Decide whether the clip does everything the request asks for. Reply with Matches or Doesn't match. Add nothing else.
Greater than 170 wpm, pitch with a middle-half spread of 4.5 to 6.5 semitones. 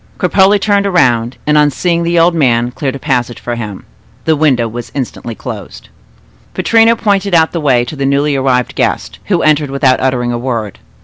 Matches